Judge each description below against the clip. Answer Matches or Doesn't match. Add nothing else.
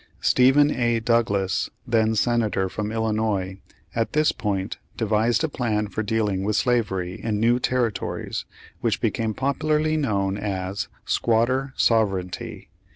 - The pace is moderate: Doesn't match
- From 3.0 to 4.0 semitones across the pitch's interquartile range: Matches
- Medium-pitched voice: Doesn't match